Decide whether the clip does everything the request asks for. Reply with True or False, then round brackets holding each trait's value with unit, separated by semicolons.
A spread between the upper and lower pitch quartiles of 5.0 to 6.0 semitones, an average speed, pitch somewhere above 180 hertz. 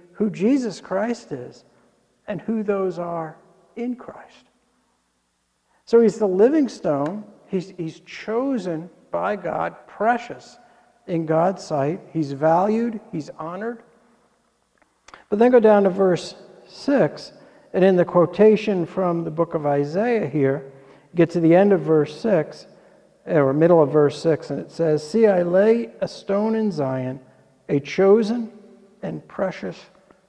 True (5.3 semitones; 145 wpm; 190 Hz)